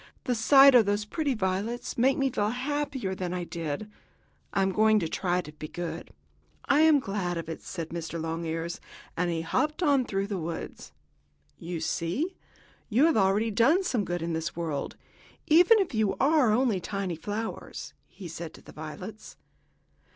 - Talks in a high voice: Yes, high, 200 Hz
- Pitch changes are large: Yes, wide, 7.1 semitones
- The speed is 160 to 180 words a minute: Yes, average, 175 wpm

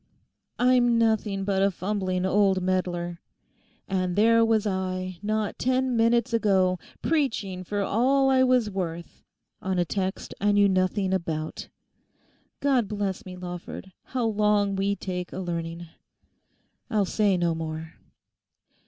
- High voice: Yes, high, 195 Hz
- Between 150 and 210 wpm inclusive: No, slow, 135 wpm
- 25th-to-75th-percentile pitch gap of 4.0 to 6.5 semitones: No, average, 3.3 semitones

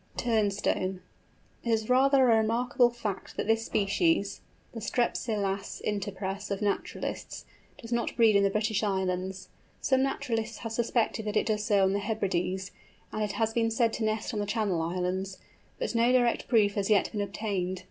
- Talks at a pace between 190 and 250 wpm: No, average, 175 wpm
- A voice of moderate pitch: No, high, 215 Hz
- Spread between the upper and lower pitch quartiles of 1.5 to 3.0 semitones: Yes, average, 2.7 semitones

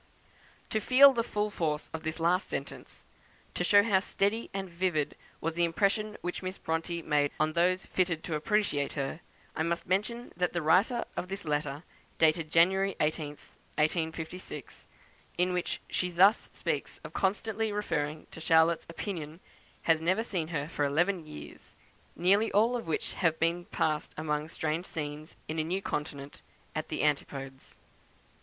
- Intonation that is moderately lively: Yes, average, 3.8 semitones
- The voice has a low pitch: No, medium, 170 Hz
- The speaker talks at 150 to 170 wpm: Yes, average, 160 wpm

